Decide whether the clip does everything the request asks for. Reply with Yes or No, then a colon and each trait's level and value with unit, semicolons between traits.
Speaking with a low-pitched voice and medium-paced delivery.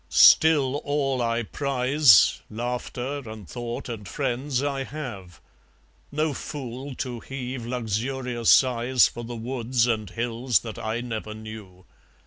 No: low, 120 Hz; slow, 125 wpm